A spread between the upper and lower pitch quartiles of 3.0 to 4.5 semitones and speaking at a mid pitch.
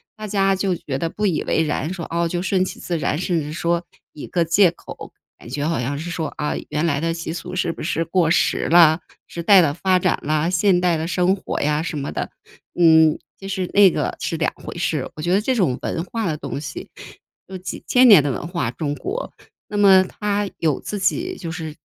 Yes: average, 3.3 semitones; medium, 170 Hz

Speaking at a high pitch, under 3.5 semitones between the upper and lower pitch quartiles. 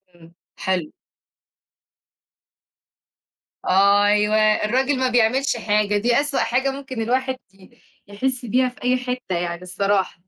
No: high, 220 Hz; average, 4.2 semitones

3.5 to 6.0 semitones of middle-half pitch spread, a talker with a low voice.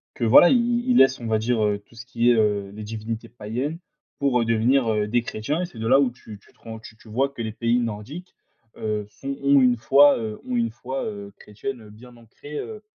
Yes: average, 3.8 semitones; low, 115 Hz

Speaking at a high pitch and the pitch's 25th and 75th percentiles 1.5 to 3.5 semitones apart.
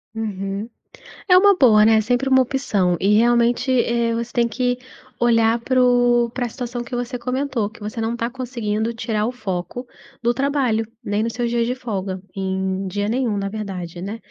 Yes: high, 230 Hz; average, 2.8 semitones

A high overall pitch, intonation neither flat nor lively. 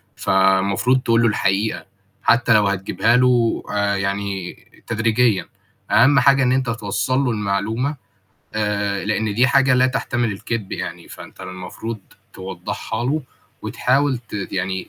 No: low, 110 Hz; average, 4.0 semitones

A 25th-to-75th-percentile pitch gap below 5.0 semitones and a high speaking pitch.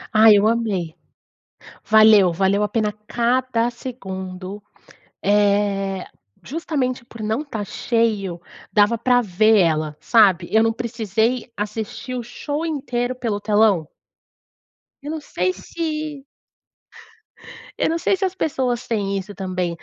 Yes: average, 3.9 semitones; high, 220 Hz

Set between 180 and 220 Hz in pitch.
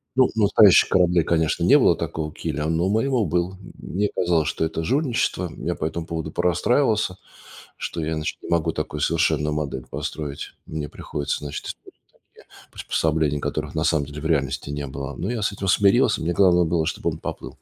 No: very low, 80 Hz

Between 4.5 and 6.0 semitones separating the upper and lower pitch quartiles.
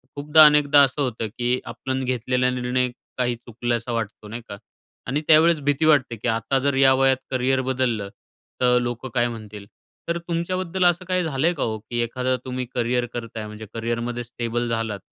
No: average, 3.1 semitones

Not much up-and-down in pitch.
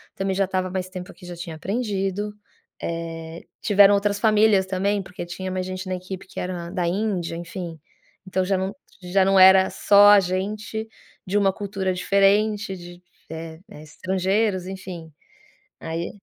Yes: narrow, 2.0 semitones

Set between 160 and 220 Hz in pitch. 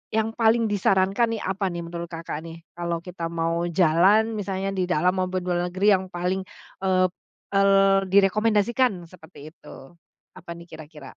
Yes: medium, 185 Hz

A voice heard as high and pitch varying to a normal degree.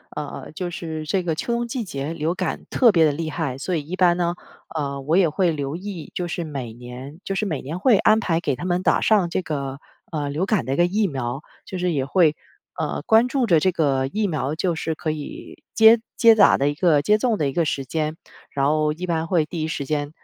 No: medium, 160 Hz; average, 4.1 semitones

